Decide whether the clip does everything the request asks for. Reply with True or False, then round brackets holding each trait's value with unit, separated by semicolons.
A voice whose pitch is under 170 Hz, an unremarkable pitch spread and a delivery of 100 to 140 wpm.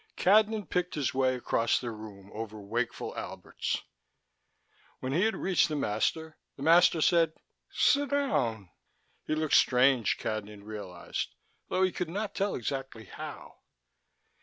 False (135 Hz; 8.3 semitones; 135 wpm)